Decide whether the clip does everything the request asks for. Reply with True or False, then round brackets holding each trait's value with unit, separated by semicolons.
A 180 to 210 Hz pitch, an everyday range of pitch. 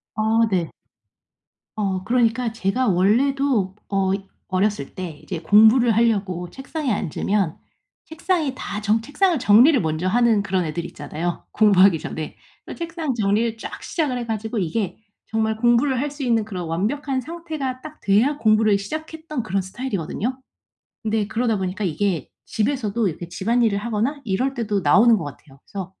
False (220 Hz; 4.9 semitones)